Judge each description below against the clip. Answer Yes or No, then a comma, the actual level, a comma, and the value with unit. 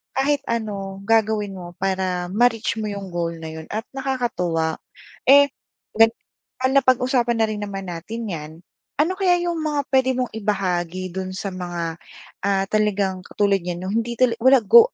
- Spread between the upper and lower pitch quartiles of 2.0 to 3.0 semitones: No, average, 5.2 semitones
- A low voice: No, high, 210 Hz